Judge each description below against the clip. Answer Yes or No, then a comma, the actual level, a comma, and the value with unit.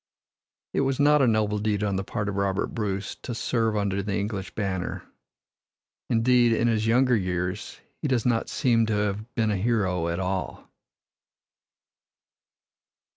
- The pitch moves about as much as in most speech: Yes, average, 3.0 semitones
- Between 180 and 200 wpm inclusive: No, average, 155 wpm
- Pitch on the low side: Yes, low, 105 Hz